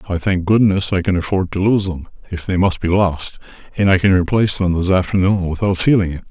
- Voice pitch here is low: Yes, very low, 95 Hz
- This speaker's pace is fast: Yes, fast, 230 wpm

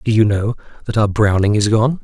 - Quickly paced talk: Yes, fast, 235 wpm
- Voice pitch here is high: No, low, 110 Hz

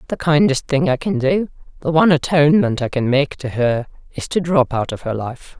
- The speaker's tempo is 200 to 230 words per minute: Yes, fast, 205 wpm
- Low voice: No, medium, 150 Hz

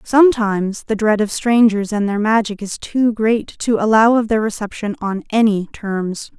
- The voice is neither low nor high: No, high, 215 Hz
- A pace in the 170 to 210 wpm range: Yes, average, 180 wpm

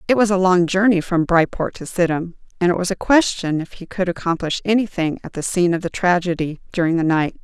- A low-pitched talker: No, medium, 180 Hz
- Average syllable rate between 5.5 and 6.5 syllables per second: Yes, 5.9 syllables/s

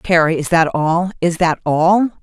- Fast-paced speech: No, average, 160 wpm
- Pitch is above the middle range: No, medium, 170 Hz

